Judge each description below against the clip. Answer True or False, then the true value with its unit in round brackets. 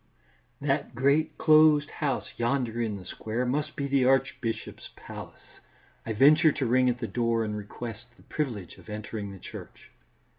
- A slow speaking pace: False (160 wpm)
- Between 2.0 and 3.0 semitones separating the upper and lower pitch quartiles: False (4.0 semitones)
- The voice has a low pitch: True (125 Hz)